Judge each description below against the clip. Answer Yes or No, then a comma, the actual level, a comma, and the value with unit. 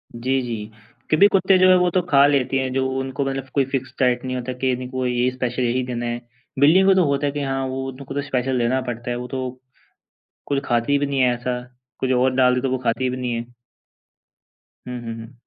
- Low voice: Yes, low, 130 Hz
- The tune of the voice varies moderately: No, narrow, 1.8 semitones